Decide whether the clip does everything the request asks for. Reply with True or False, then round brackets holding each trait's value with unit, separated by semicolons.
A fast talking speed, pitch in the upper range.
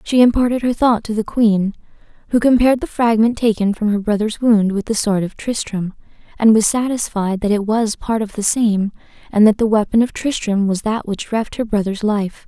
True (210 wpm; 215 Hz)